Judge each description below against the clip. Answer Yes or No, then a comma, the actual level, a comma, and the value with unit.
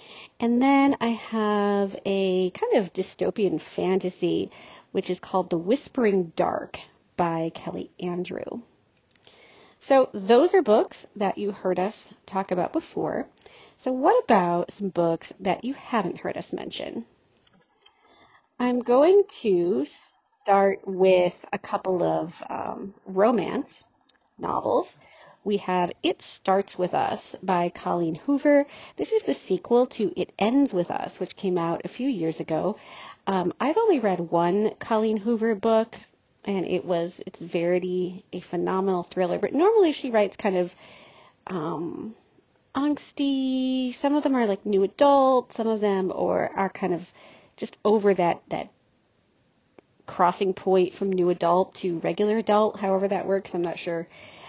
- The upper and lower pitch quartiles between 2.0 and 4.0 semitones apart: No, wide, 5.4 semitones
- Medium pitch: No, high, 195 Hz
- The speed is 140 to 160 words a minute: Yes, average, 145 wpm